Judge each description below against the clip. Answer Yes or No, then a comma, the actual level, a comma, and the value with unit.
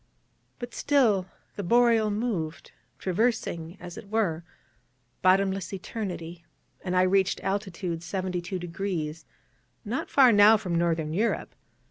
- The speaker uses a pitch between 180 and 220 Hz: Yes, high, 190 Hz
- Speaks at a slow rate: Yes, slow, 110 wpm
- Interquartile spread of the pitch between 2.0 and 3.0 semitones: No, average, 3.9 semitones